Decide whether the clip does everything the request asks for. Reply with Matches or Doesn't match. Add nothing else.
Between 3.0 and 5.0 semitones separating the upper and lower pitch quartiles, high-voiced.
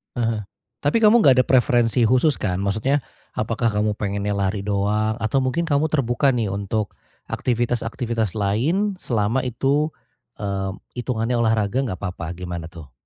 Doesn't match